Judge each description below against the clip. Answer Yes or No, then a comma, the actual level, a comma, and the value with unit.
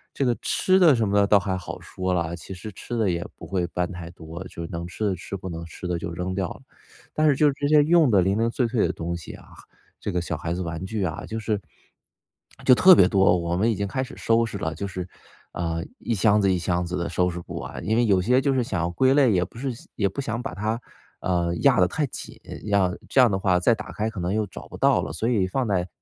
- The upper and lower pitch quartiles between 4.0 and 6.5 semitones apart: Yes, average, 4.7 semitones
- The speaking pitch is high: No, very low, 95 Hz